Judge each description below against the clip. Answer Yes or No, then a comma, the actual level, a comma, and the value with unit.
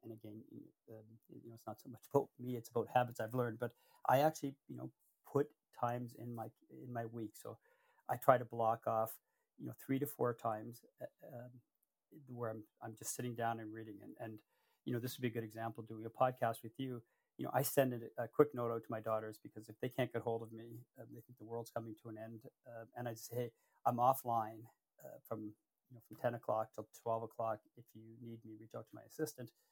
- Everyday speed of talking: No, fast, 235 wpm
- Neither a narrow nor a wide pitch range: No, narrow, 1.7 semitones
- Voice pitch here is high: No, low, 115 Hz